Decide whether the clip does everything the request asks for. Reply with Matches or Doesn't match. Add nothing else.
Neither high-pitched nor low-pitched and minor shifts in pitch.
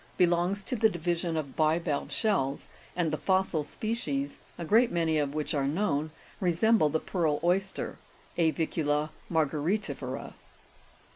Doesn't match